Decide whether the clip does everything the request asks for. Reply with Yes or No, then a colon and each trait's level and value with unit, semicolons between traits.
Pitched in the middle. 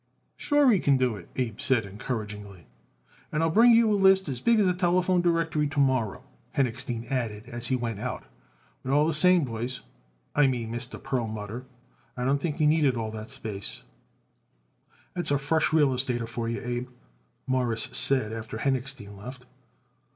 No: low, 130 Hz